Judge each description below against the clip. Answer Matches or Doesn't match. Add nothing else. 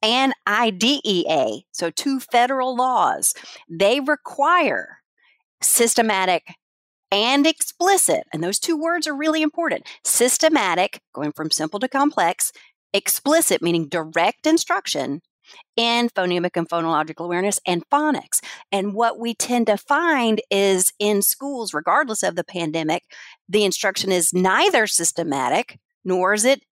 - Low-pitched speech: Doesn't match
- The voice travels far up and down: Matches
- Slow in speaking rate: Matches